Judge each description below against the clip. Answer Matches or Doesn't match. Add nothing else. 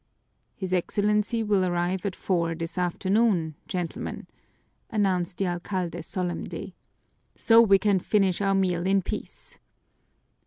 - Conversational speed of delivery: Doesn't match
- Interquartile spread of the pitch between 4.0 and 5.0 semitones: Doesn't match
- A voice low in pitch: Doesn't match